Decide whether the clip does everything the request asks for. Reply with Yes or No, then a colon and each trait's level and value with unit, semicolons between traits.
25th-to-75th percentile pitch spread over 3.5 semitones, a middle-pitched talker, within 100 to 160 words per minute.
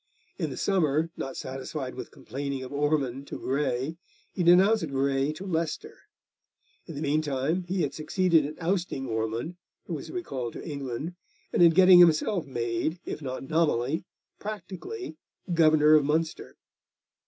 Yes: average, 4.2 semitones; medium, 155 Hz; average, 145 wpm